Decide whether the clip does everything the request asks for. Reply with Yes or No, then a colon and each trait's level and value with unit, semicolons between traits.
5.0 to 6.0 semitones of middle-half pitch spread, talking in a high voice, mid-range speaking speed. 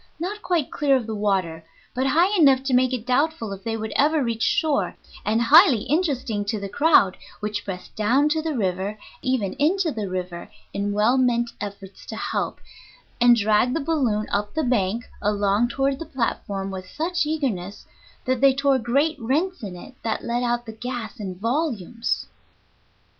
Yes: average, 5.3 semitones; high, 240 Hz; average, 180 wpm